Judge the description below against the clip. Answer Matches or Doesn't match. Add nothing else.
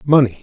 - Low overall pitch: Matches